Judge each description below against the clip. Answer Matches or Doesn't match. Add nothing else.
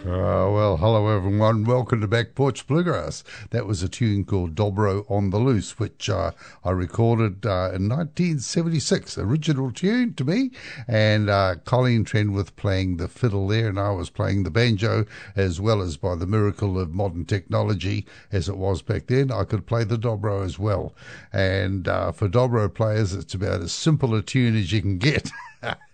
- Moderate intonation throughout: Matches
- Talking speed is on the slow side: Doesn't match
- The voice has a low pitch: Matches